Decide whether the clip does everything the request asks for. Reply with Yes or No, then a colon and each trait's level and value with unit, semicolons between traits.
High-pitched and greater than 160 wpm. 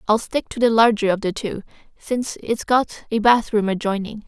Yes: high, 220 Hz; average, 195 wpm